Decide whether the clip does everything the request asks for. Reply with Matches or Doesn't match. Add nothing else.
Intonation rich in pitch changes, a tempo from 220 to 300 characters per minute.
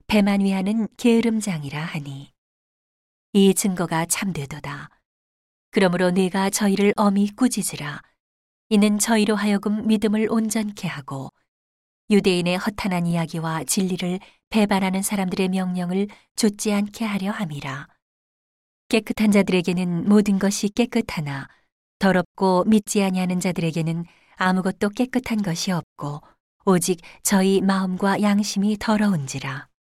Doesn't match